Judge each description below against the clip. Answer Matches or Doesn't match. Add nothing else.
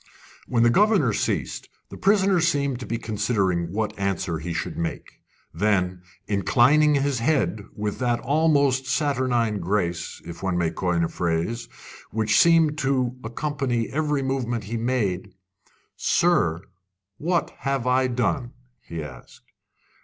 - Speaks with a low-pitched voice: Matches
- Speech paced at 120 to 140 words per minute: Matches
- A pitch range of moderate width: Doesn't match